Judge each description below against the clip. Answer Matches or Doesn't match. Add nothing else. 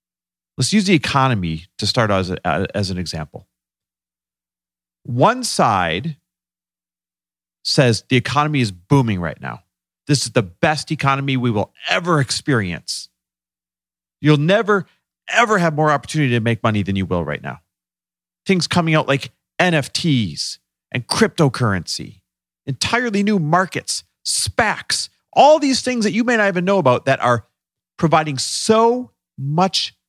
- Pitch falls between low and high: Doesn't match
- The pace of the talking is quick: Doesn't match